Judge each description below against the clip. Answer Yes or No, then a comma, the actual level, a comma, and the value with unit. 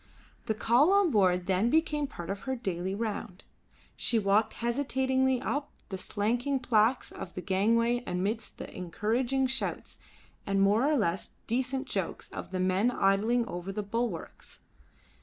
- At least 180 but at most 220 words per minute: No, average, 150 wpm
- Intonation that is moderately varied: Yes, average, 4.9 semitones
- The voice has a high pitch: Yes, high, 225 Hz